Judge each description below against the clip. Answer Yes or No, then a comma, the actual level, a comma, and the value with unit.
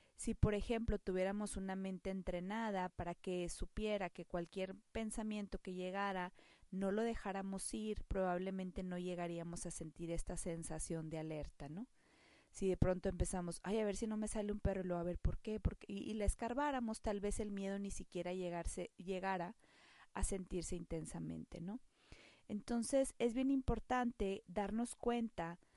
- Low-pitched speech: No, high, 195 Hz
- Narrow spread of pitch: No, average, 3.3 semitones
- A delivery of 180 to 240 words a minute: No, average, 170 wpm